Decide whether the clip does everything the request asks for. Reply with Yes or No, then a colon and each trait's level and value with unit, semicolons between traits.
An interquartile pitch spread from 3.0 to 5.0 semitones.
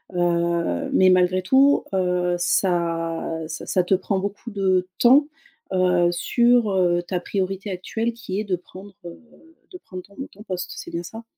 No: narrow, 2.5 semitones